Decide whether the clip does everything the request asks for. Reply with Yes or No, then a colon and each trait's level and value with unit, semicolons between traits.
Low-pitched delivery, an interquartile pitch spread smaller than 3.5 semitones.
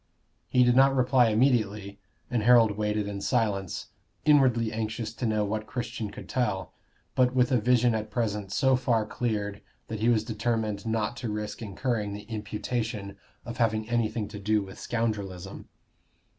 Yes: low, 110 Hz; narrow, 2.5 semitones